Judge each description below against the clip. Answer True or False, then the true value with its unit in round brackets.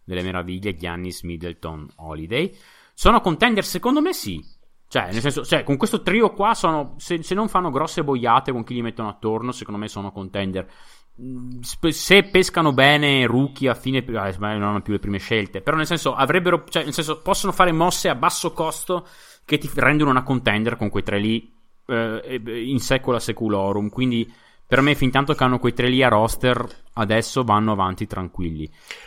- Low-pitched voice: True (125 Hz)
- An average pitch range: False (7.0 semitones)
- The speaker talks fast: True (185 wpm)